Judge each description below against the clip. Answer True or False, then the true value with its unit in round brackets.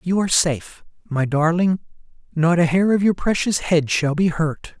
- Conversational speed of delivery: True (190 wpm)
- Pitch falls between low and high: True (170 Hz)